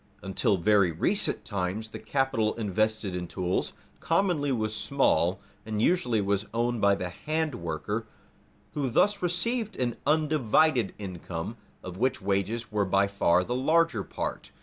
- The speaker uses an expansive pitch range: Yes, wide, 6.4 semitones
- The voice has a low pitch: Yes, low, 110 Hz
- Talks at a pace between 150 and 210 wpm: No, average, 140 wpm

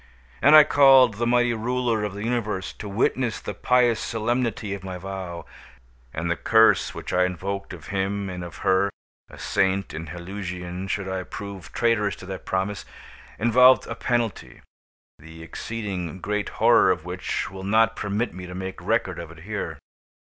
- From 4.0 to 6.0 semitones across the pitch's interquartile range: No, average, 3.6 semitones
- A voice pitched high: No, low, 100 Hz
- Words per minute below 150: No, average, 170 wpm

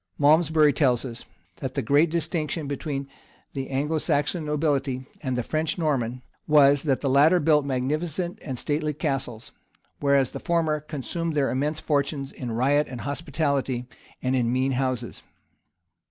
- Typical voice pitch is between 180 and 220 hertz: No, medium, 145 Hz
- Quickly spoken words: No, average, 155 wpm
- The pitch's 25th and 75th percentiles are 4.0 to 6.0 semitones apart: No, average, 2.7 semitones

